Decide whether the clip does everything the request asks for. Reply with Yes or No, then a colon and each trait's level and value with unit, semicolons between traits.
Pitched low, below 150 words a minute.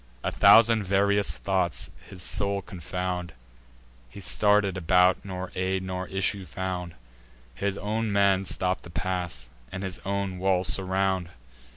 Yes: very low, 95 Hz; slow, 135 wpm